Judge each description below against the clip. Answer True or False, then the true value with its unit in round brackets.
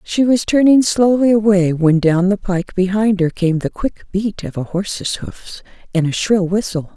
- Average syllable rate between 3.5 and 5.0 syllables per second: True (4.5 syllables/s)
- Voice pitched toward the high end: True (195 Hz)